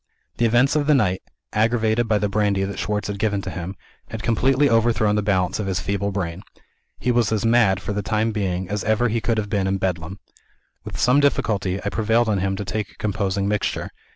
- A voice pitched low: Yes, low, 105 Hz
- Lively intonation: No, average, 2.7 semitones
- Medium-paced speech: No, fast, 220 wpm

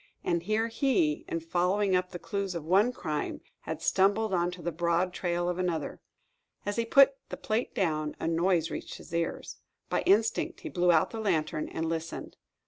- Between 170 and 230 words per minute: Yes, average, 185 wpm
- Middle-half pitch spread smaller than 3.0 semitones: No, average, 3.9 semitones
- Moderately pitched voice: Yes, medium, 180 Hz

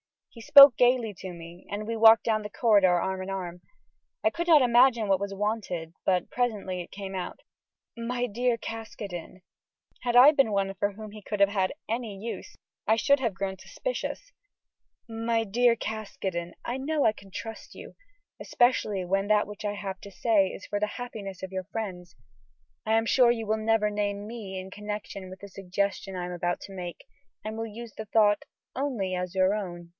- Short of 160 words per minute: No, average, 195 wpm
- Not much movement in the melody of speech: No, average, 3.2 semitones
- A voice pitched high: Yes, high, 210 Hz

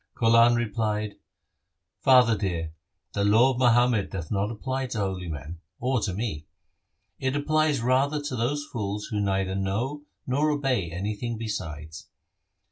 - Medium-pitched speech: No, low, 115 Hz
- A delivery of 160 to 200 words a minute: No, average, 140 wpm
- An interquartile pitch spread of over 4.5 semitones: Yes, average, 4.9 semitones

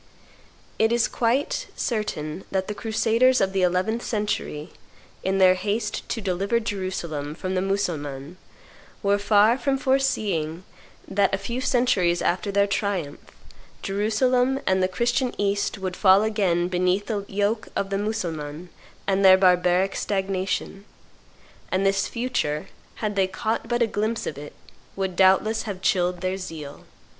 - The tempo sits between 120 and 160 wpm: Yes, average, 145 wpm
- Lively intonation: No, average, 3.1 semitones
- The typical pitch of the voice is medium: No, high, 195 Hz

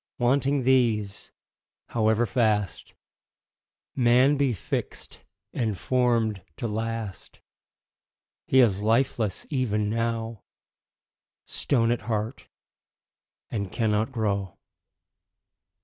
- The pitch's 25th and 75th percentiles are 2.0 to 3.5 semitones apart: Yes, average, 2.7 semitones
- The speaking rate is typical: No, slow, 85 wpm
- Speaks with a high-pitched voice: No, low, 115 Hz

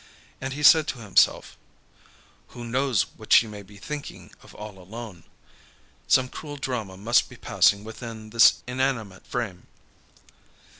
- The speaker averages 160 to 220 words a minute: No, average, 140 wpm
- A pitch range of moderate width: Yes, average, 4.1 semitones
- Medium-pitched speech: No, low, 115 Hz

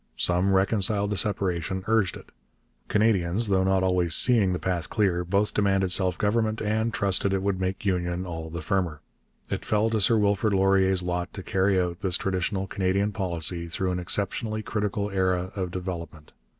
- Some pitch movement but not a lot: No, narrow, 2.2 semitones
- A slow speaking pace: No, average, 175 wpm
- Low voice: Yes, very low, 95 Hz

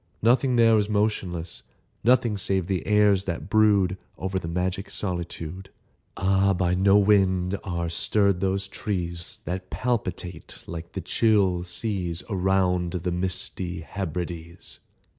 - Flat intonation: Yes, narrow, 2.3 semitones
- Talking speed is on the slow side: Yes, slow, 125 wpm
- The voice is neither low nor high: No, very low, 95 Hz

